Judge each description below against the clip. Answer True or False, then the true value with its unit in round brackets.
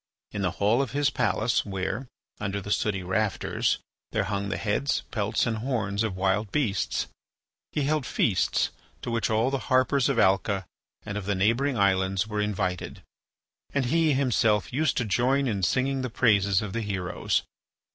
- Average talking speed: True (170 wpm)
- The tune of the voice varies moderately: True (4.5 semitones)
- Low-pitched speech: True (110 Hz)